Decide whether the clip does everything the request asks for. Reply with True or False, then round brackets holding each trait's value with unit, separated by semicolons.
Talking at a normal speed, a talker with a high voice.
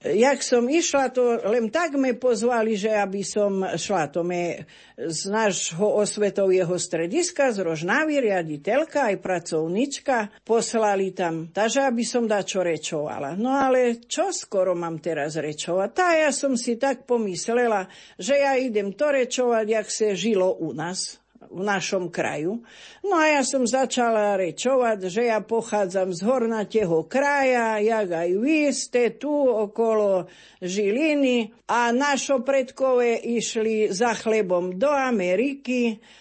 True (140 wpm; 225 Hz)